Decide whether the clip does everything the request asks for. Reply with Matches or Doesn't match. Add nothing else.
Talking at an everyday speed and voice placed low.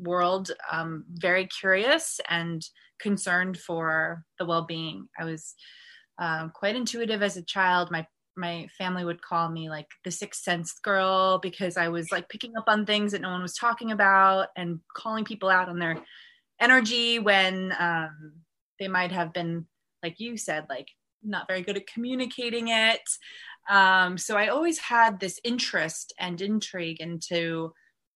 Doesn't match